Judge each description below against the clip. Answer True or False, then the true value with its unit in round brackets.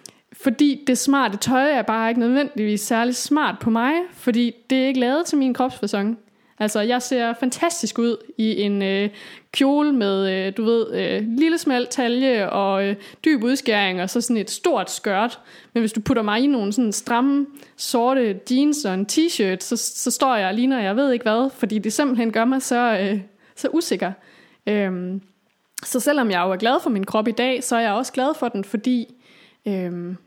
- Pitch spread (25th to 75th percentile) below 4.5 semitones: True (3.9 semitones)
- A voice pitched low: False (235 Hz)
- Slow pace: False (200 wpm)